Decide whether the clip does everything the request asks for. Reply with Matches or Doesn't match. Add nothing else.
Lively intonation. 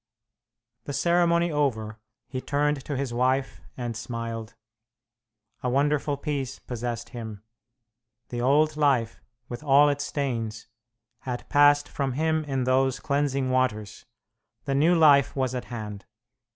Doesn't match